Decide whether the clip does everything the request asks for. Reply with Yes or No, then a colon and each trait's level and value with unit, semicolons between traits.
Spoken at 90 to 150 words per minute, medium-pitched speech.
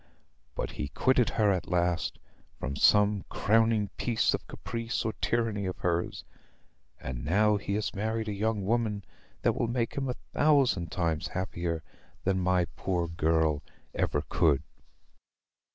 No: average, 145 wpm; low, 100 Hz